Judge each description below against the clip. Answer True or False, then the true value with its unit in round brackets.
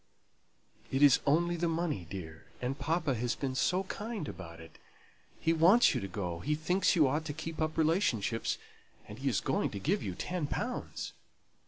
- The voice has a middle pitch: True (150 Hz)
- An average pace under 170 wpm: False (185 wpm)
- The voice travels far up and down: True (7.1 semitones)